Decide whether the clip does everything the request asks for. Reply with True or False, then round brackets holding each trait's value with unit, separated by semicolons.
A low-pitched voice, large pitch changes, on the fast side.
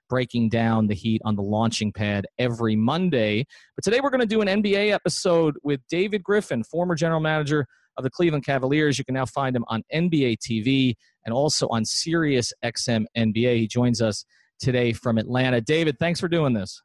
False (130 Hz; 5.8 semitones; 190 wpm)